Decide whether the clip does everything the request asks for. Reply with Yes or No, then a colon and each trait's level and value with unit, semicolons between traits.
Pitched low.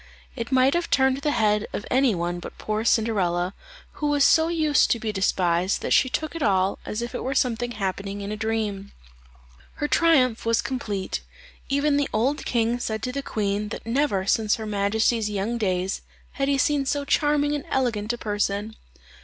No: high, 225 Hz